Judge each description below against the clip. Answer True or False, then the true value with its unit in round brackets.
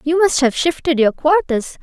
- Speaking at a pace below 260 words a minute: True (200 wpm)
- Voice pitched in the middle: False (300 Hz)